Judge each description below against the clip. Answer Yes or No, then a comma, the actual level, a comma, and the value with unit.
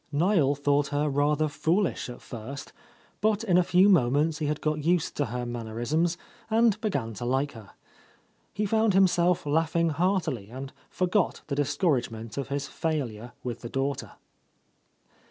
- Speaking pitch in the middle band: Yes, medium, 145 Hz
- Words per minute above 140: Yes, average, 155 wpm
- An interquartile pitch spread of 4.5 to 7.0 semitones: Yes, average, 5.2 semitones